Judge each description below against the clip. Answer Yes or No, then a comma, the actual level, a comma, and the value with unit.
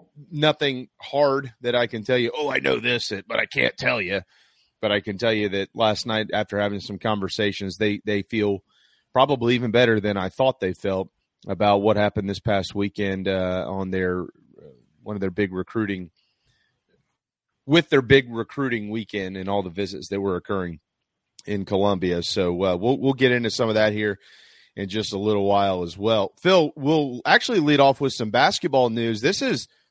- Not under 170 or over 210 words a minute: Yes, average, 195 wpm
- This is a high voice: No, low, 105 Hz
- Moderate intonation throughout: Yes, average, 3.8 semitones